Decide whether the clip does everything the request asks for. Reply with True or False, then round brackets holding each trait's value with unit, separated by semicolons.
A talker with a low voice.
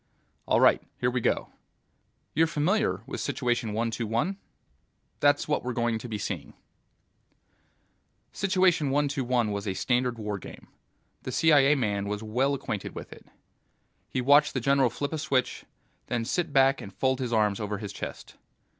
True (125 Hz)